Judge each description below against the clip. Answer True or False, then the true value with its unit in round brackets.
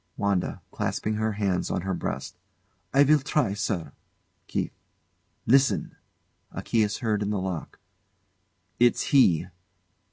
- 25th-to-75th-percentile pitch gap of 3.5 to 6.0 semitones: True (4.3 semitones)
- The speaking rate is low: True (130 wpm)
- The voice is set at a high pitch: False (105 Hz)